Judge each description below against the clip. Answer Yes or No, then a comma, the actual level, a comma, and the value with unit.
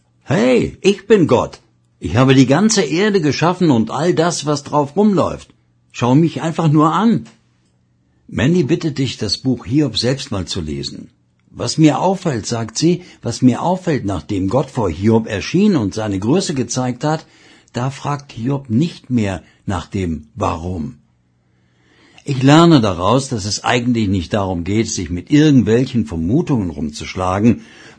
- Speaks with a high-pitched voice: No, low, 120 Hz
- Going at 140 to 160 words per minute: Yes, average, 150 wpm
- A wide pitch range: Yes, wide, 8.1 semitones